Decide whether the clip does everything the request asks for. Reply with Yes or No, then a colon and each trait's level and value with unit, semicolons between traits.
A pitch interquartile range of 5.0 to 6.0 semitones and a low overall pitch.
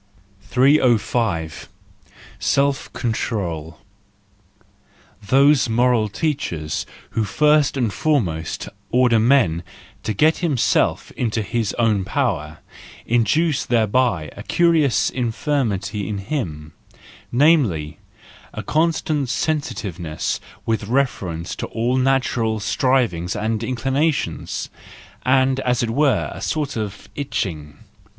Yes: wide, 5.6 semitones; low, 120 Hz